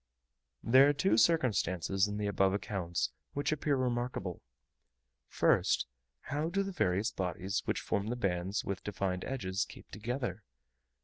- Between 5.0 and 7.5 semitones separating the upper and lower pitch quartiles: Yes, wide, 5.6 semitones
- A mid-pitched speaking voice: No, low, 105 Hz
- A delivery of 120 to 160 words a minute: Yes, average, 140 wpm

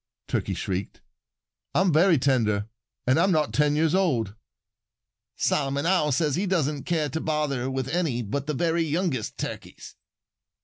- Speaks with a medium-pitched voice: Yes, medium, 150 Hz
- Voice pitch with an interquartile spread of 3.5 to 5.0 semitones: Yes, average, 4.0 semitones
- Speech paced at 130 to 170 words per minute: Yes, average, 145 wpm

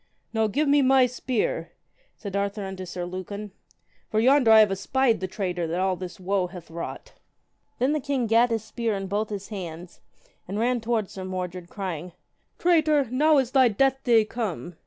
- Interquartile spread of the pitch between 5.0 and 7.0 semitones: Yes, average, 5.3 semitones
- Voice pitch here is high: Yes, high, 215 Hz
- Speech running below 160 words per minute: No, average, 185 wpm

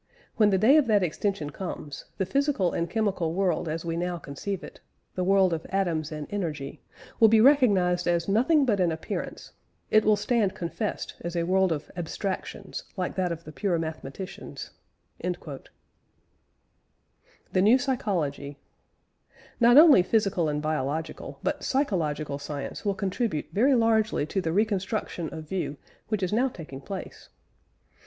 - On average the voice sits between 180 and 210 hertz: Yes, medium, 185 Hz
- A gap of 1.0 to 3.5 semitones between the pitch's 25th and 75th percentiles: No, average, 4.8 semitones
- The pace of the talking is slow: No, average, 150 wpm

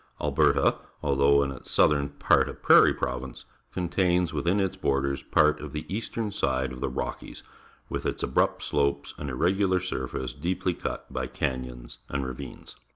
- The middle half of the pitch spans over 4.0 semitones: Yes, average, 5.2 semitones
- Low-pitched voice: Yes, very low, 70 Hz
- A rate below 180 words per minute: Yes, average, 160 wpm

